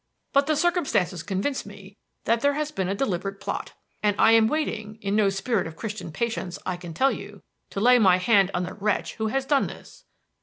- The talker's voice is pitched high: Yes, high, 210 Hz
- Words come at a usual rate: No, fast, 215 wpm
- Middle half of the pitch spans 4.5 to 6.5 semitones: Yes, average, 5.1 semitones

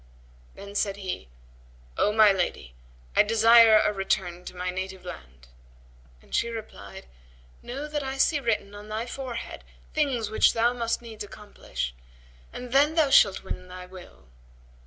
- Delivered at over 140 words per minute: Yes, average, 155 wpm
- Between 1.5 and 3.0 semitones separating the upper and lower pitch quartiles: No, average, 4.3 semitones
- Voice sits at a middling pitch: No, high, 215 Hz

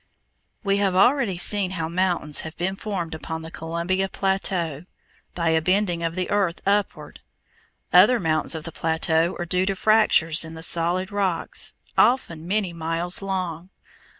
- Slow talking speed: No, average, 155 wpm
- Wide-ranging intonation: No, average, 3.0 semitones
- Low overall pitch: No, medium, 175 Hz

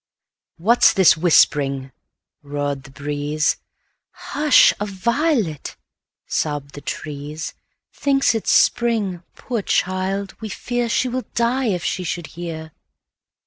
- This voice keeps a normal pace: No, slow, 105 wpm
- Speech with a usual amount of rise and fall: No, wide, 7.9 semitones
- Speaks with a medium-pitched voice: Yes, medium, 180 Hz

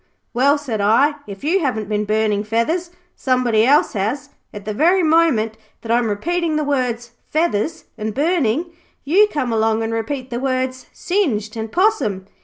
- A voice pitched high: Yes, very high, 250 Hz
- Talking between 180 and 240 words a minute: No, average, 165 wpm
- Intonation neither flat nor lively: No, wide, 5.8 semitones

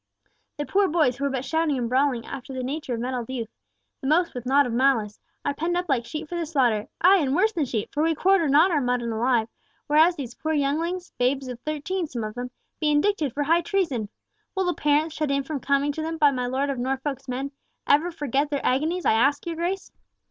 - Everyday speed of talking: No, fast, 220 wpm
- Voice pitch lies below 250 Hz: No, very high, 285 Hz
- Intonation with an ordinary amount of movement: Yes, average, 4.2 semitones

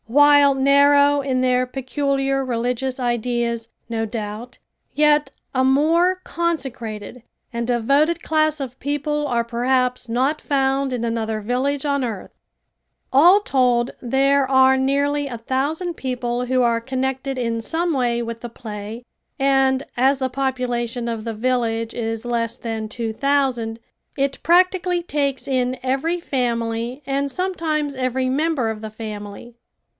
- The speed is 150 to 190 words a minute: No, average, 140 wpm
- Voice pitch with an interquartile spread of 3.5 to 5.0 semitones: No, average, 3.1 semitones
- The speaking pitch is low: No, very high, 260 Hz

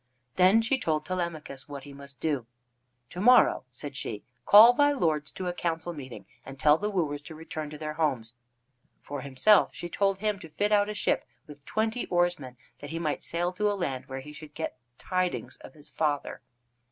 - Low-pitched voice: No, medium, 160 Hz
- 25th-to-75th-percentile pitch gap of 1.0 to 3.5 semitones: No, average, 4.6 semitones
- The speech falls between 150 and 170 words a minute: No, average, 200 wpm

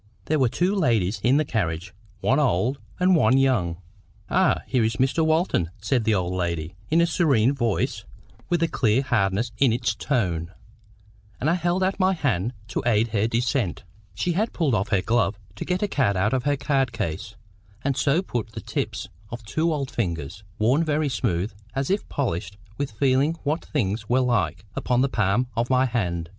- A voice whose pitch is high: No, low, 120 Hz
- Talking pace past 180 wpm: Yes, average, 190 wpm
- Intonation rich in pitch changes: Yes, wide, 6.0 semitones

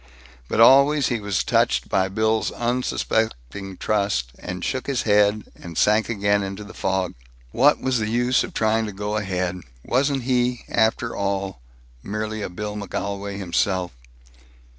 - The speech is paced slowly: No, average, 150 wpm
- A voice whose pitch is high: No, low, 105 Hz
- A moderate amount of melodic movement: Yes, average, 3.2 semitones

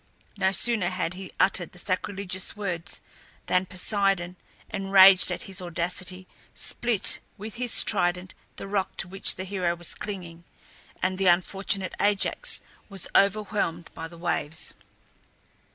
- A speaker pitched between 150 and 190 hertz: Yes, medium, 185 Hz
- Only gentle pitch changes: Yes, narrow, 2.0 semitones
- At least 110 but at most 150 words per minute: Yes, slow, 135 wpm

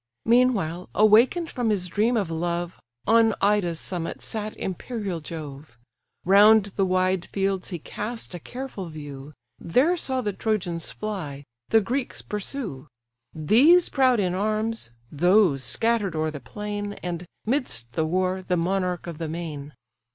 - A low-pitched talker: No, high, 190 Hz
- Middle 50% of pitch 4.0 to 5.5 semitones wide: Yes, average, 4.7 semitones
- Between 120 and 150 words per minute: Yes, average, 145 wpm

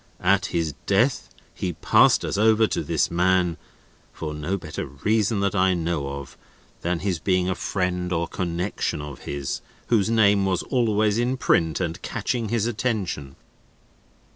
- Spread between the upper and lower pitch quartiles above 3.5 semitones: Yes, average, 4.2 semitones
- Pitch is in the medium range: No, very low, 95 Hz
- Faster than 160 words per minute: No, average, 155 wpm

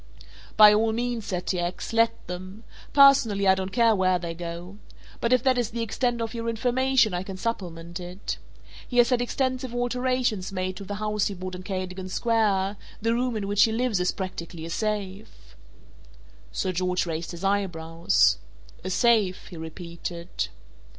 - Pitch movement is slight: No, average, 4.3 semitones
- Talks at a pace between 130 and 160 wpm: No, average, 175 wpm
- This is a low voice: No, high, 200 Hz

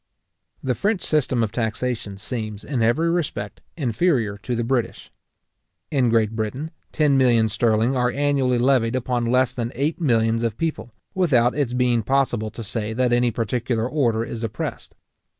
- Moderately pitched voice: No, low, 120 Hz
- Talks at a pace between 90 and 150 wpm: No, average, 160 wpm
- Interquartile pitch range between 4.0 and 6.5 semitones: No, average, 2.8 semitones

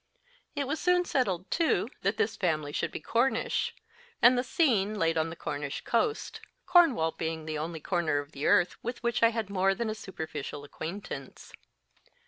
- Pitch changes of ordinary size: No, wide, 7.4 semitones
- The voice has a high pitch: Yes, high, 195 Hz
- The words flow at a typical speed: Yes, average, 175 wpm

